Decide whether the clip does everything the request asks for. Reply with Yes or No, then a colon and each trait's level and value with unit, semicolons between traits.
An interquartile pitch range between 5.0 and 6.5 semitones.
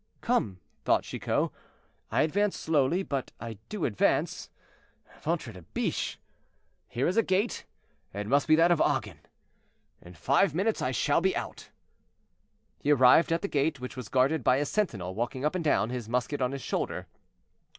Yes: wide, 5.4 semitones